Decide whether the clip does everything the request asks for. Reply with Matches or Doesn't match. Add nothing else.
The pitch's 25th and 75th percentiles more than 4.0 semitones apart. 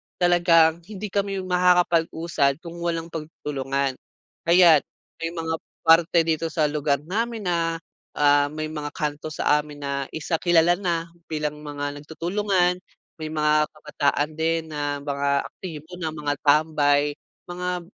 Doesn't match